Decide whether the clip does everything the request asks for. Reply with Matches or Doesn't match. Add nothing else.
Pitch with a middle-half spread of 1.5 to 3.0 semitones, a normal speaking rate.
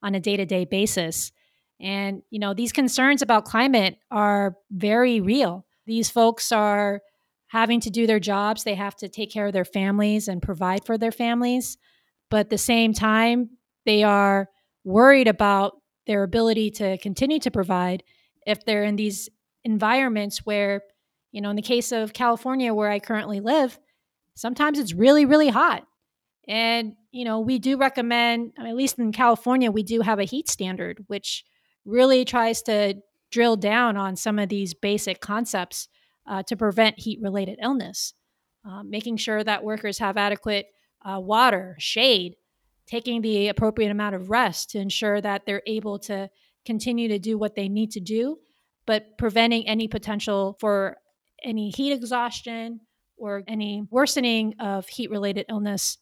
Matches